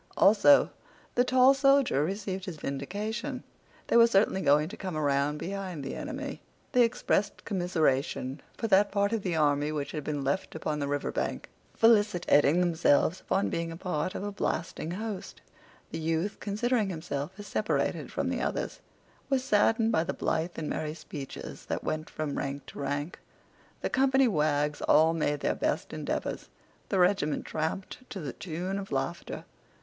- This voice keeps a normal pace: Yes, average, 170 wpm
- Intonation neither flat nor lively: No, wide, 5.7 semitones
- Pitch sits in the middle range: Yes, medium, 180 Hz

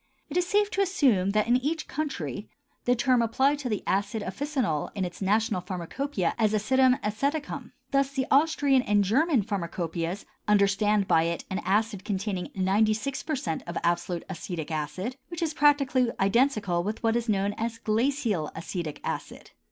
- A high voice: Yes, high, 215 Hz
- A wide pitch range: Yes, wide, 6.1 semitones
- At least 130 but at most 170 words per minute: Yes, average, 160 wpm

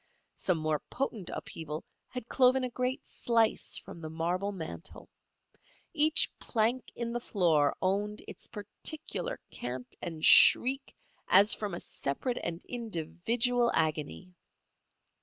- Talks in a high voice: Yes, high, 205 Hz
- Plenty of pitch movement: Yes, wide, 6.9 semitones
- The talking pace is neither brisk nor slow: No, slow, 120 wpm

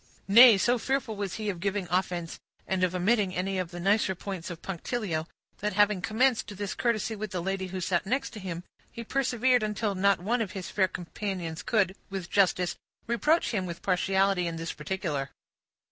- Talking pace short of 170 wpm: No, average, 185 wpm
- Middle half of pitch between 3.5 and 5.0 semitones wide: No, average, 3.0 semitones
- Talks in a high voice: Yes, high, 195 Hz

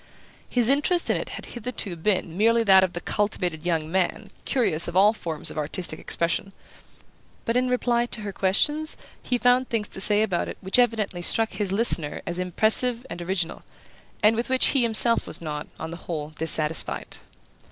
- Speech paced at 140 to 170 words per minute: No, average, 185 wpm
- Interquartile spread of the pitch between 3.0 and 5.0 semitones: No, wide, 5.4 semitones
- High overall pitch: Yes, high, 200 Hz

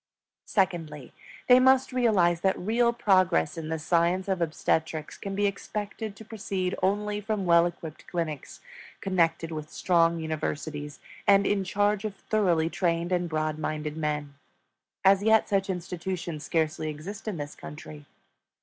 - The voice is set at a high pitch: No, medium, 175 Hz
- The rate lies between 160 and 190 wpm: No, average, 145 wpm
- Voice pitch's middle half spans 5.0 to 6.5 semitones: No, average, 4.2 semitones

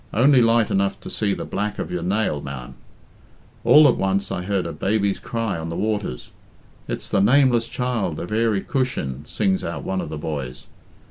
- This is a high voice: No, low, 100 Hz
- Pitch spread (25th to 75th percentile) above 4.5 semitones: Yes, average, 5.1 semitones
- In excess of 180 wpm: Yes, average, 190 wpm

